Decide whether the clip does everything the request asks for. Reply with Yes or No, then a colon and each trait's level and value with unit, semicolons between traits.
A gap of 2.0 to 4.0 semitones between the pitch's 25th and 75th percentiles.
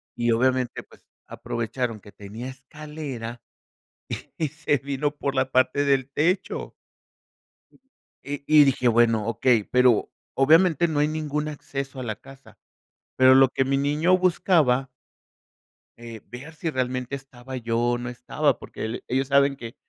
Yes: average, 3.3 semitones